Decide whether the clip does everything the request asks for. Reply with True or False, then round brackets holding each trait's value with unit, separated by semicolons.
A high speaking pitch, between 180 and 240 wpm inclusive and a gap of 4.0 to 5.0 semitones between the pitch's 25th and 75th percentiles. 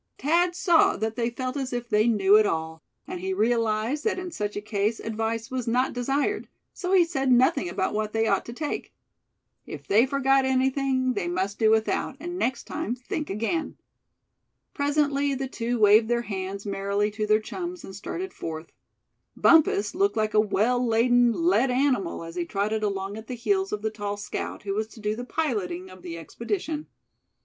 True (230 Hz; 190 wpm; 4.6 semitones)